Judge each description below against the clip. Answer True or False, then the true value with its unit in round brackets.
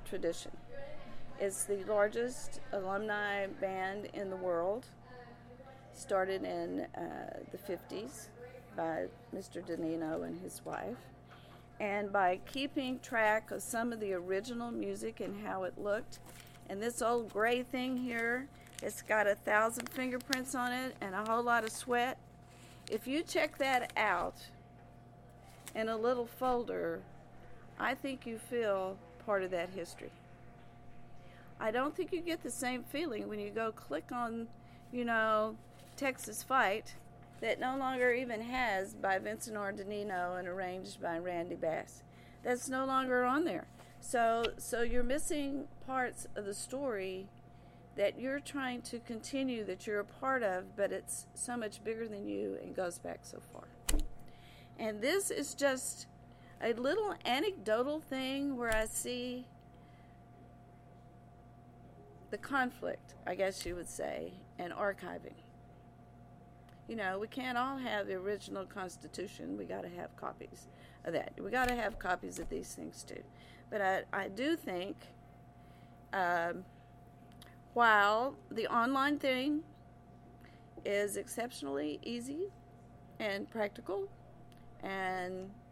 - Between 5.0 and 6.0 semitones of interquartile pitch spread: True (5.3 semitones)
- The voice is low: False (215 Hz)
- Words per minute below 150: True (135 wpm)